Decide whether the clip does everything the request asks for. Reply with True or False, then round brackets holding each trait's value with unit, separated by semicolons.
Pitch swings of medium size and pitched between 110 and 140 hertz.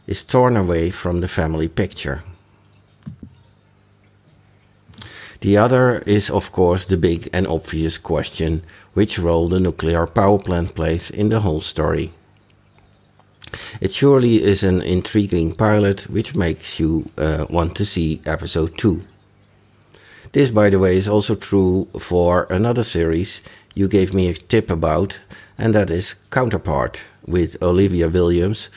False (3.5 semitones; 95 Hz)